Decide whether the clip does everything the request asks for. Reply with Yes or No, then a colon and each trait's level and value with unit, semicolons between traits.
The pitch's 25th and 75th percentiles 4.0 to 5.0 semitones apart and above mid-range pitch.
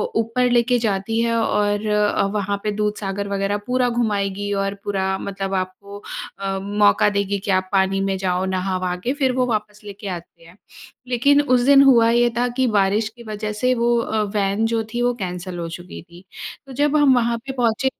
No: average, 3.5 semitones; high, 210 Hz